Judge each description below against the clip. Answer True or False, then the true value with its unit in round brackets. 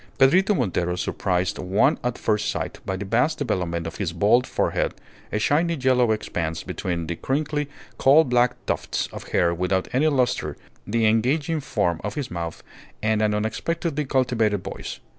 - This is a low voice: True (110 Hz)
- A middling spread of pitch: False (6.4 semitones)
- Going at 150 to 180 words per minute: True (160 wpm)